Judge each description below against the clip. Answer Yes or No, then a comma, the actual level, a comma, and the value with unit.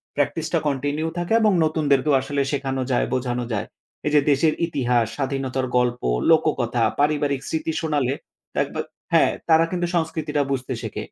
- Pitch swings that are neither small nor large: Yes, average, 3.2 semitones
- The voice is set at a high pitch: No, medium, 145 Hz